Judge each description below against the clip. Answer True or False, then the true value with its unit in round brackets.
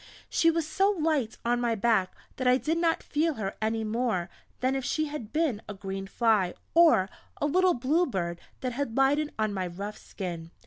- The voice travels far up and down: True (6.9 semitones)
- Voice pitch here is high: True (240 Hz)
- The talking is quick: False (195 wpm)